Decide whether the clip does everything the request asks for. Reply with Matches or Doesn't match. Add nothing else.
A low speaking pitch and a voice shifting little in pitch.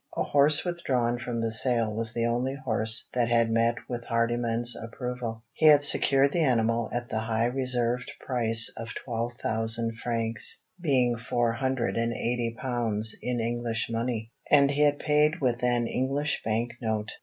Matches